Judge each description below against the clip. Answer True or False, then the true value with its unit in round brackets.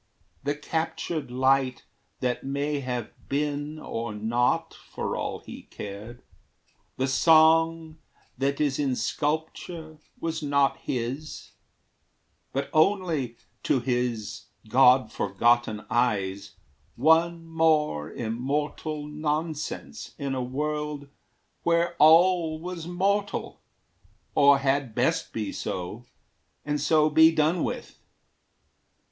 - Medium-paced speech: False (105 wpm)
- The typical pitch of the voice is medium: True (145 Hz)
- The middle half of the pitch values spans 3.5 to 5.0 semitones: True (4.2 semitones)